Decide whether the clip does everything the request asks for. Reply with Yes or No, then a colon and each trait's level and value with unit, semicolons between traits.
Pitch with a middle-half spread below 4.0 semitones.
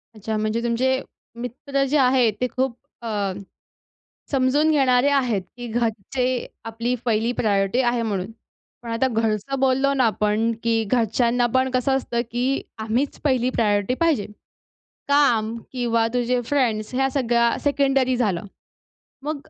Yes: average, 2.8 semitones